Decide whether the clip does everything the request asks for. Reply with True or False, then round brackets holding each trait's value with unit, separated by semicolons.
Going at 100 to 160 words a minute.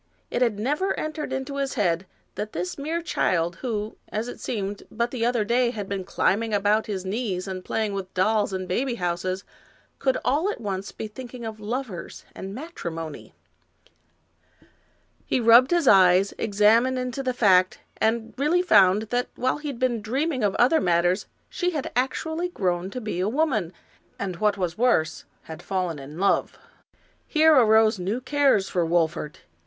False (170 wpm)